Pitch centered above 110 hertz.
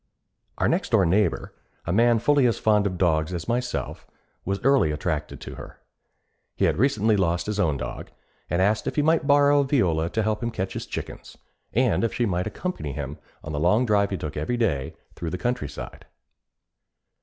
No: low, 100 Hz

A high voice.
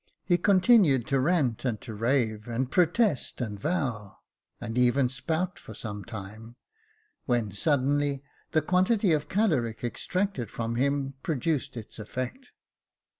No: low, 130 Hz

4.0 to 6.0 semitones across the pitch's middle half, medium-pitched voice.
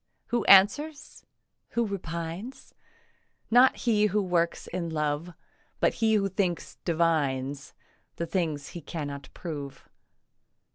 Yes: average, 5.2 semitones; medium, 170 Hz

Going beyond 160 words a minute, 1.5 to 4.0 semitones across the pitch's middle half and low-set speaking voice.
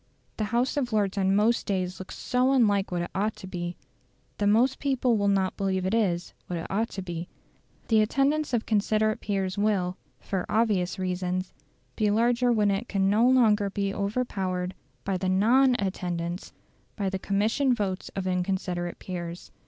No: average, 175 wpm; average, 3.2 semitones; high, 200 Hz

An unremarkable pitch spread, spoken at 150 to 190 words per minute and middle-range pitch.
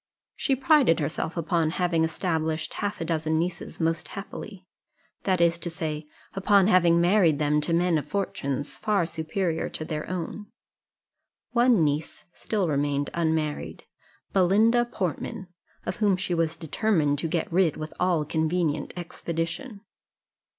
No: average, 3.3 semitones; average, 140 wpm; medium, 170 Hz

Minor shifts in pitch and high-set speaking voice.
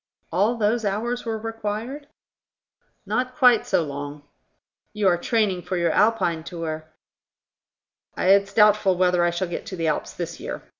No: average, 4.6 semitones; high, 200 Hz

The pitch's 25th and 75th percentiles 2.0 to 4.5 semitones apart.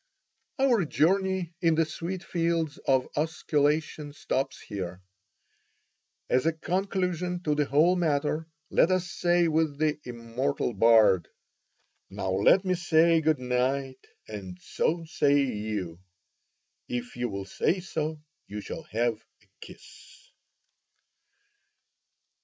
No: wide, 5.6 semitones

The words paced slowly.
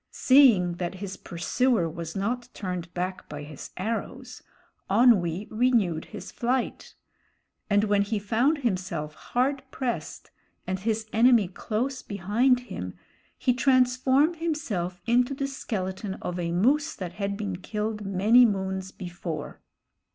Yes: slow, 130 wpm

